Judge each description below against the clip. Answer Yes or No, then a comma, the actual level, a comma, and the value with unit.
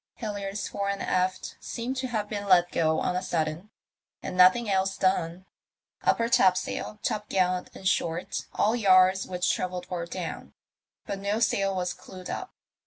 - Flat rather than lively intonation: Yes, narrow, 2.1 semitones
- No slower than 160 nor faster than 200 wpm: Yes, average, 165 wpm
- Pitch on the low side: No, high, 190 Hz